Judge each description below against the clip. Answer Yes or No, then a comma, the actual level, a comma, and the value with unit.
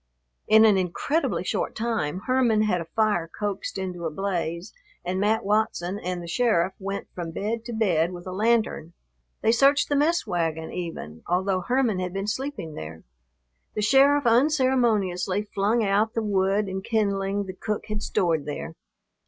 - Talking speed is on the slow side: No, average, 165 wpm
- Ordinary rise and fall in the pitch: Yes, average, 3.9 semitones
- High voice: Yes, high, 200 Hz